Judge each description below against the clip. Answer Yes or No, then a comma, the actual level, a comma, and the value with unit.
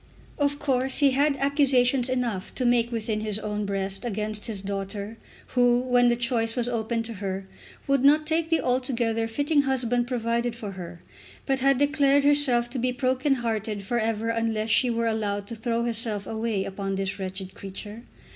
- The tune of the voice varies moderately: Yes, average, 3.3 semitones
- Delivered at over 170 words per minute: Yes, average, 180 wpm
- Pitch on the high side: Yes, high, 235 Hz